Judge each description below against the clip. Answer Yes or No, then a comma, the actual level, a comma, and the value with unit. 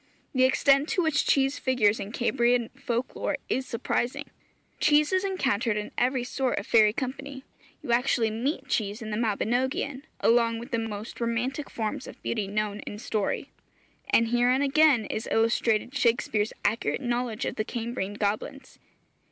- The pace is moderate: Yes, average, 160 wpm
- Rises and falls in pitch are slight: No, average, 3.3 semitones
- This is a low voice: No, high, 240 Hz